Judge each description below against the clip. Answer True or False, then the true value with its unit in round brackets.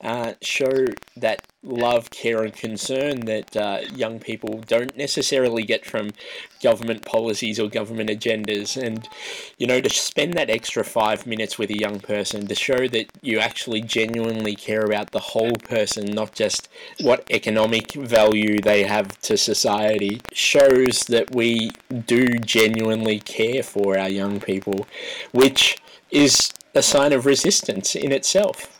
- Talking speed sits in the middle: True (150 wpm)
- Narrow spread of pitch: True (2.0 semitones)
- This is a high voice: False (110 Hz)